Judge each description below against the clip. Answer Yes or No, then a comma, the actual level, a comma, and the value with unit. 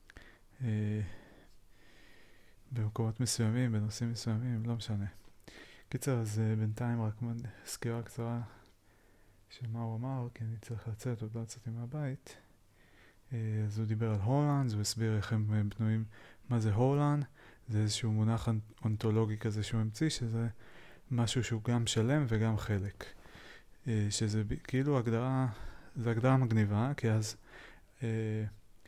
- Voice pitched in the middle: No, low, 110 Hz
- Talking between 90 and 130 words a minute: No, average, 140 wpm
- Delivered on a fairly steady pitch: Yes, narrow, 1.9 semitones